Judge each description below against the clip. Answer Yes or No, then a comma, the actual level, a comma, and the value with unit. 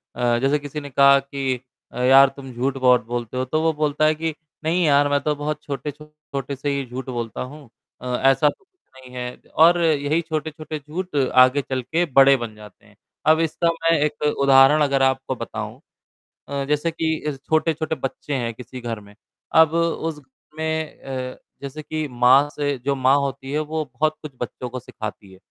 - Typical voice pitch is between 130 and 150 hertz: Yes, medium, 140 Hz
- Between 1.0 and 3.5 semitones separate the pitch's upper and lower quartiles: Yes, average, 3.0 semitones